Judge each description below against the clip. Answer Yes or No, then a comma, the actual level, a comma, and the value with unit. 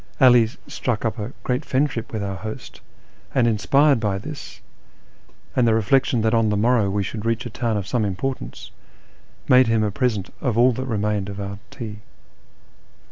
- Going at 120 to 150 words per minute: No, average, 180 wpm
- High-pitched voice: No, low, 115 Hz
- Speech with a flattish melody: No, average, 3.3 semitones